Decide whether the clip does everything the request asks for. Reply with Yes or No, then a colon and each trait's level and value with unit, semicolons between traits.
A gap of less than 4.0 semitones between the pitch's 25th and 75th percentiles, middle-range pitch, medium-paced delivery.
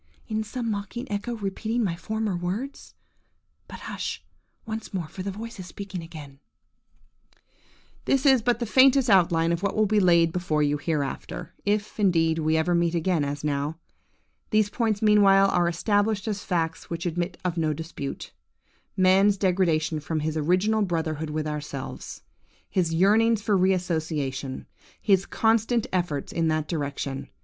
No: average, 4.6 semitones; medium, 180 Hz; average, 155 wpm